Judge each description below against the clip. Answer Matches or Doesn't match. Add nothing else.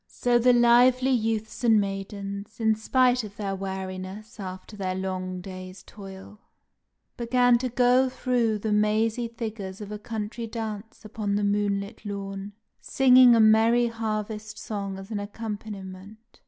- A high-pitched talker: Matches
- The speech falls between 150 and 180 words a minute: Doesn't match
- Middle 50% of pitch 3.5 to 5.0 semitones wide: Doesn't match